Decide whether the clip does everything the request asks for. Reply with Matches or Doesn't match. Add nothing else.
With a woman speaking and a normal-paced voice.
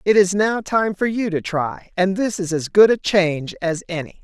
Doesn't match